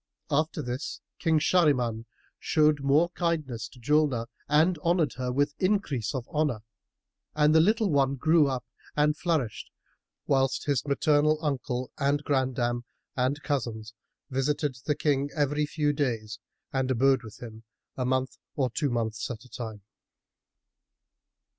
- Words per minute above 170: No, average, 140 wpm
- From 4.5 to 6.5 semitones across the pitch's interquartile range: No, average, 3.4 semitones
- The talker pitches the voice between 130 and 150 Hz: Yes, medium, 140 Hz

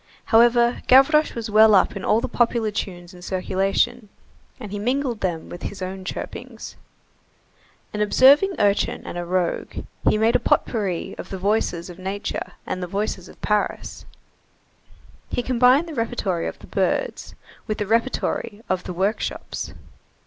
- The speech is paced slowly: No, average, 155 wpm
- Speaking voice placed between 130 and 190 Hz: No, high, 210 Hz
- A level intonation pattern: No, average, 4.1 semitones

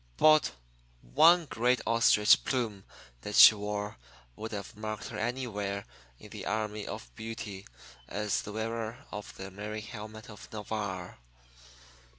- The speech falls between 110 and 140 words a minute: Yes, slow, 135 wpm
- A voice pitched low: Yes, low, 105 Hz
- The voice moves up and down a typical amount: No, narrow, 1.7 semitones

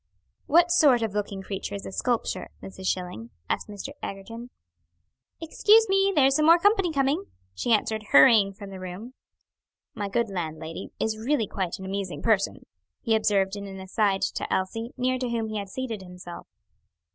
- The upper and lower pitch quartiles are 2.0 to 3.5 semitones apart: No, average, 4.9 semitones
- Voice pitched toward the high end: Yes, high, 210 Hz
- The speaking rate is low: No, average, 170 wpm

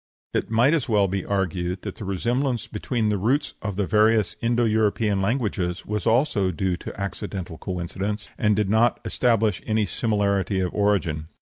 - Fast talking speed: No, average, 165 wpm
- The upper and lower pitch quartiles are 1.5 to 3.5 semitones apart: Yes, average, 2.8 semitones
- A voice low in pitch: Yes, low, 105 Hz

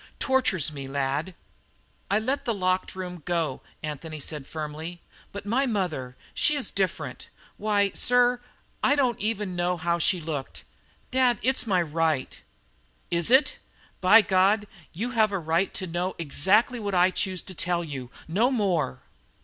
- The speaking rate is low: No, average, 155 wpm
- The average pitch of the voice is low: No, medium, 185 Hz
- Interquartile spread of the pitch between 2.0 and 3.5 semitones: No, average, 5.1 semitones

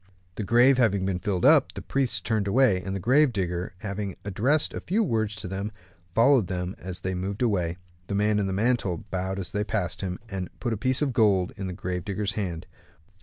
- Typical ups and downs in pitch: Yes, average, 3.6 semitones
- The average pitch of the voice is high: No, low, 100 Hz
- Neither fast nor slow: No, fast, 220 wpm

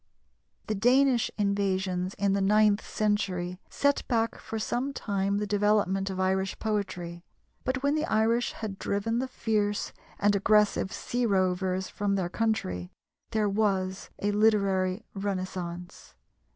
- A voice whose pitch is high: Yes, high, 200 Hz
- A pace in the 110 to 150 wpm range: Yes, slow, 135 wpm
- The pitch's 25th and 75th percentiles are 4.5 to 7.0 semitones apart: No, narrow, 2.4 semitones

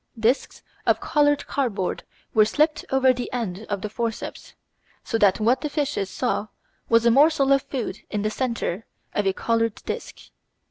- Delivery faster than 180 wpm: No, average, 170 wpm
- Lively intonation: No, average, 4.2 semitones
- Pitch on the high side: Yes, high, 230 Hz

